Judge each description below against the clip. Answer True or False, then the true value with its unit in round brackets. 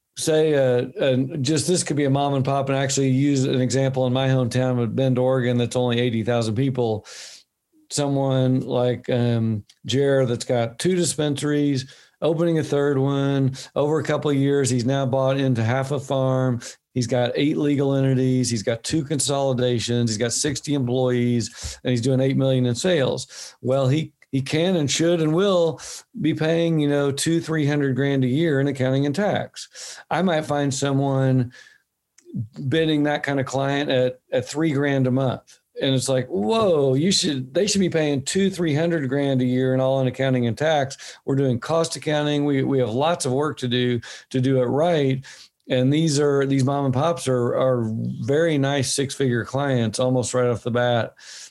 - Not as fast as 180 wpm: False (190 wpm)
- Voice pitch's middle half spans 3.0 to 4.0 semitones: False (2.5 semitones)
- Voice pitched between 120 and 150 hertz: True (135 Hz)